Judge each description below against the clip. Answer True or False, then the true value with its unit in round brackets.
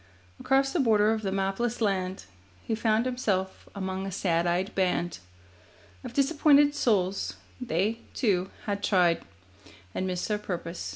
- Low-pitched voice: False (200 Hz)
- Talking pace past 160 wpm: False (140 wpm)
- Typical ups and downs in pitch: True (3.9 semitones)